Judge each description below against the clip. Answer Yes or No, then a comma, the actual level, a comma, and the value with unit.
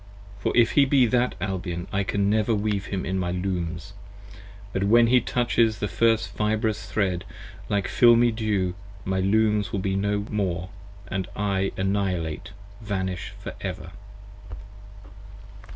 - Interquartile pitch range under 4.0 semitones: Yes, narrow, 2.6 semitones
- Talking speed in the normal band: Yes, average, 145 wpm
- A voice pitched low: Yes, low, 100 Hz